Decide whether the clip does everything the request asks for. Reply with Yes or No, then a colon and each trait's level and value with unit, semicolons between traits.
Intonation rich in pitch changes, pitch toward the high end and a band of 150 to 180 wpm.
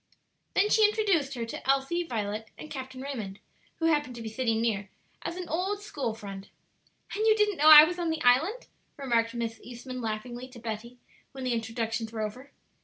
No: wide, 6.0 semitones; very high, 255 Hz; average, 190 wpm